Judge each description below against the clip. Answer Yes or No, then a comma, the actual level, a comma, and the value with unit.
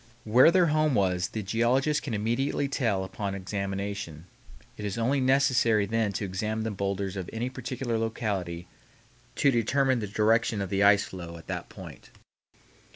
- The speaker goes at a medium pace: Yes, average, 160 wpm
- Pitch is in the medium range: No, low, 110 Hz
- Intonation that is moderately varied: Yes, average, 4.3 semitones